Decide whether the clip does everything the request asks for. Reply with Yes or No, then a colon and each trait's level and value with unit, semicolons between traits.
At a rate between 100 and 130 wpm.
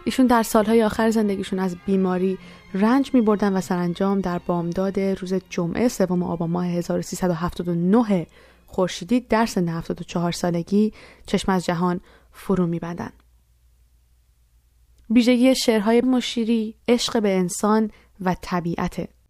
Yes: average, 120 wpm